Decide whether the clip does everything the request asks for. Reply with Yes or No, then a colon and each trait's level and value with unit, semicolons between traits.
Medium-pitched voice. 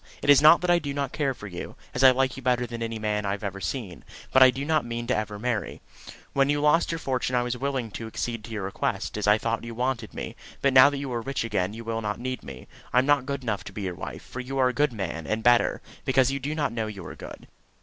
No: low, 125 Hz